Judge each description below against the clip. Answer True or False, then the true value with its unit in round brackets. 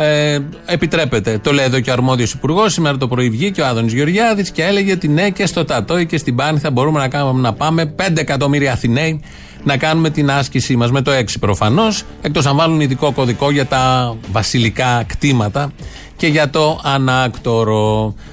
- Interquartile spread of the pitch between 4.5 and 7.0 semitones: False (4.0 semitones)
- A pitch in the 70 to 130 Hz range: False (140 Hz)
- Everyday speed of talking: False (185 wpm)